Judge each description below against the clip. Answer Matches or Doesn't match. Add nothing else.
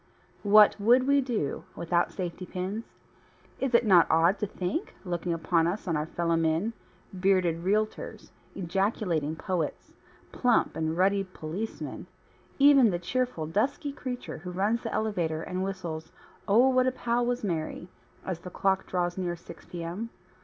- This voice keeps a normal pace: Matches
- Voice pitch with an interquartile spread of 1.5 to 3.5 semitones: Doesn't match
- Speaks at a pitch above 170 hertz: Matches